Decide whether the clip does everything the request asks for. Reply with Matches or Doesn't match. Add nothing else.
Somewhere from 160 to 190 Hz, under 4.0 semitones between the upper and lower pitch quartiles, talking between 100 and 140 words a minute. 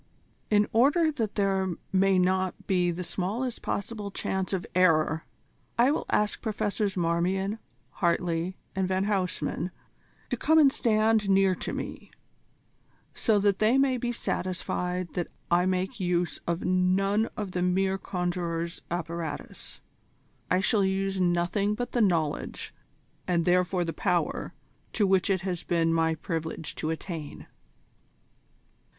Matches